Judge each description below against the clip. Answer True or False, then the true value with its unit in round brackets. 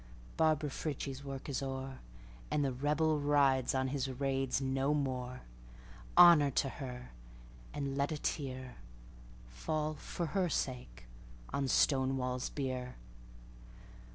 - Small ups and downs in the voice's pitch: True (2.3 semitones)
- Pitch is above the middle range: False (135 Hz)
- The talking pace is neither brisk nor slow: False (105 wpm)